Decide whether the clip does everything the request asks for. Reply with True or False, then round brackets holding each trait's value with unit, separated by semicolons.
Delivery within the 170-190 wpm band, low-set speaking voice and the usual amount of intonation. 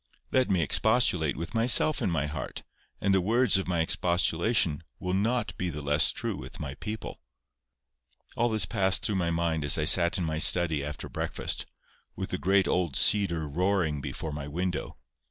True (180 wpm; 90 Hz; 4.1 semitones)